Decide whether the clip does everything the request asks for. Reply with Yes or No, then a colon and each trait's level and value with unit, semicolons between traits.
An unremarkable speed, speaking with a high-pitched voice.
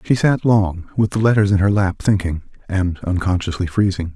No: average, 175 wpm; very low, 95 Hz